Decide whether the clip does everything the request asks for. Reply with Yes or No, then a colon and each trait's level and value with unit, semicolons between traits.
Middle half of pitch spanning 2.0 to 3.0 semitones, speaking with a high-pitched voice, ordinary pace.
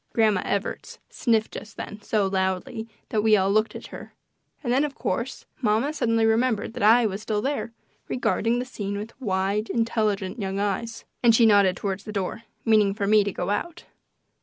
Yes: narrow, 2.4 semitones; high, 215 Hz; average, 185 wpm